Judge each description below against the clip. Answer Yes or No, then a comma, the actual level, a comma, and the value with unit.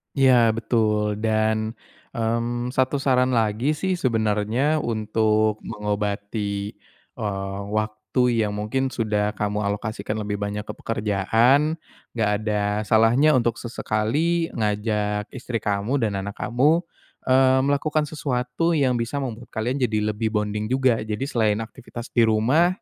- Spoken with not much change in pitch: No, average, 3.4 semitones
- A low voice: Yes, low, 110 Hz